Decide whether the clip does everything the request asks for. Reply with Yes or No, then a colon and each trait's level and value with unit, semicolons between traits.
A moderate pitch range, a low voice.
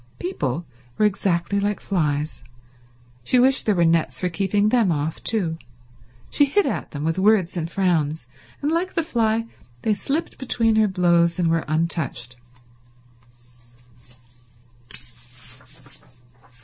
No: average, 5.0 semitones; medium, 185 Hz